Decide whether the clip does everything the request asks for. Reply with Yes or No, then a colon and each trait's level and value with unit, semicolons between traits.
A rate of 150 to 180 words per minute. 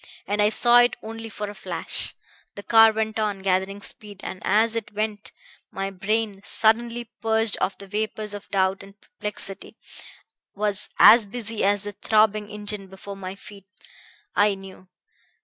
Yes: average, 160 wpm